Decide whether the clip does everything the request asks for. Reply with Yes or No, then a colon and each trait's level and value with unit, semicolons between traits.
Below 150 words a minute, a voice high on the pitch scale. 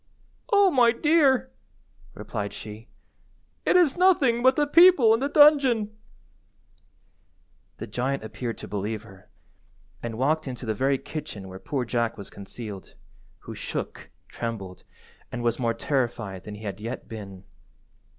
No: average, 140 wpm; low, 125 Hz